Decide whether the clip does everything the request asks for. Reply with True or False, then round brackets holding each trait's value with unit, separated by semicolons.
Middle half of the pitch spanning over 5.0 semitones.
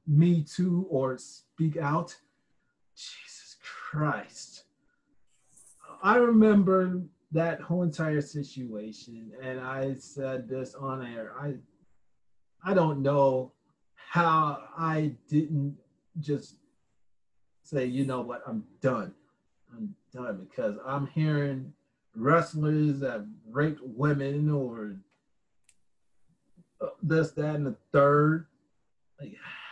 False (3.9 semitones)